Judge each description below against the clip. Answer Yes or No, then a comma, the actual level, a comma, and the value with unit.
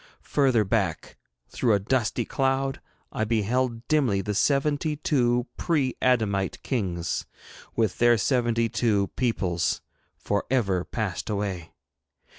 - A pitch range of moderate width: Yes, average, 4.5 semitones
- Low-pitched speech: Yes, low, 115 Hz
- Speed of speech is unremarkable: No, slow, 115 wpm